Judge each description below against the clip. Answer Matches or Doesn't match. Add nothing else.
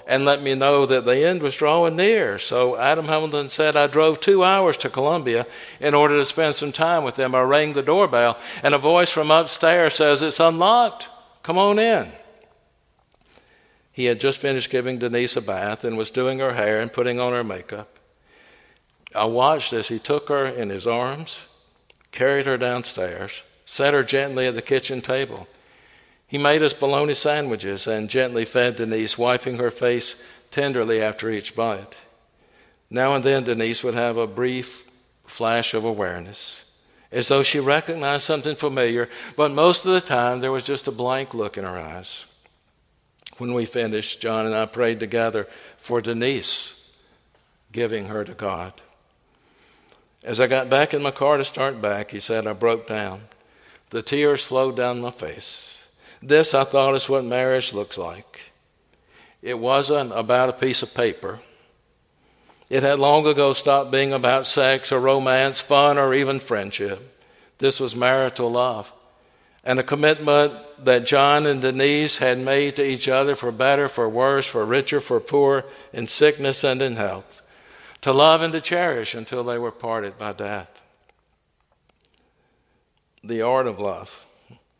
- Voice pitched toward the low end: Matches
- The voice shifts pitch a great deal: Doesn't match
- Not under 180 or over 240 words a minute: Doesn't match